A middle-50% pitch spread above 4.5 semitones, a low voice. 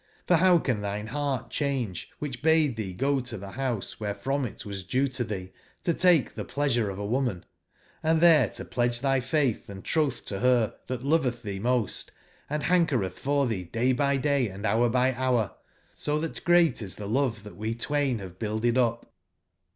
Yes: average, 4.9 semitones; low, 125 Hz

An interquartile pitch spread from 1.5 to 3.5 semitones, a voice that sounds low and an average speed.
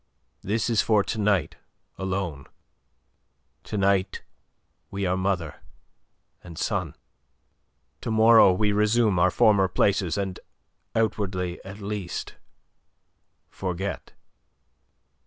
No: narrow, 2.4 semitones; low, 100 Hz; slow, 100 wpm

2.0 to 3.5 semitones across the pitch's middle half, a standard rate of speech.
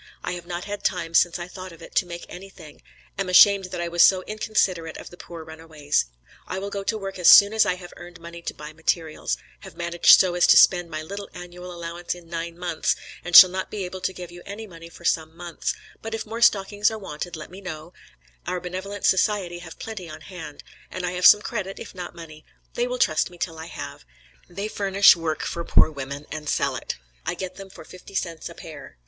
No: narrow, 2.6 semitones; fast, 235 wpm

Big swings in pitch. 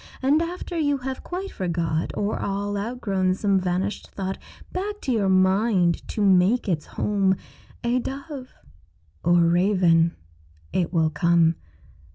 Yes: wide, 6.0 semitones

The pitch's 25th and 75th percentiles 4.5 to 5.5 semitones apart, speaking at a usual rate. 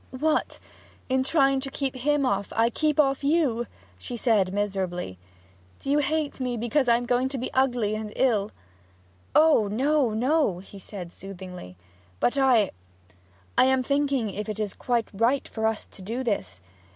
Yes: average, 4.8 semitones; average, 170 wpm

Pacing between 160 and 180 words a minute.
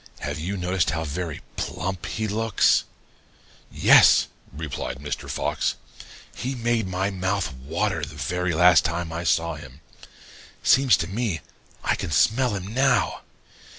No: average, 140 wpm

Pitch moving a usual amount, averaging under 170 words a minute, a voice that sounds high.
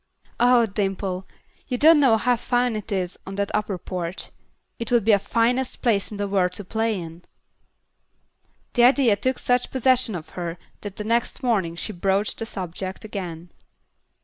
No: average, 4.2 semitones; average, 175 wpm; high, 210 Hz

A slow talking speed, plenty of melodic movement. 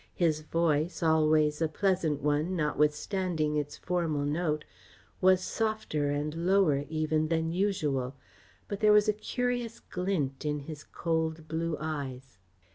No: slow, 130 wpm; average, 3.4 semitones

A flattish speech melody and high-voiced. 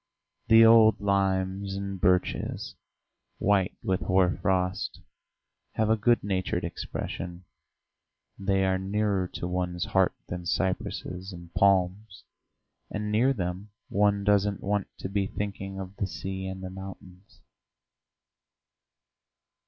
No: narrow, 1.7 semitones; very low, 95 Hz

